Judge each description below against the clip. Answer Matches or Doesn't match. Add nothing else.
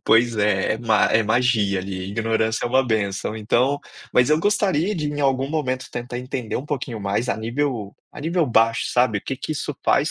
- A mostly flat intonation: Doesn't match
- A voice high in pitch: Doesn't match